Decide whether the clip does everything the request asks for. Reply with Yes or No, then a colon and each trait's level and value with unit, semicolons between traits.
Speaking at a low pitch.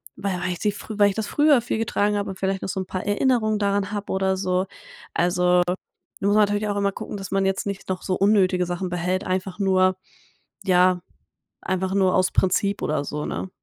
No: high, 190 Hz